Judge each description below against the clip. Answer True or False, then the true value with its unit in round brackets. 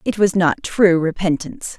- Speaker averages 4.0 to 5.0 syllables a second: True (4.7 syllables/s)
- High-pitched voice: False (180 Hz)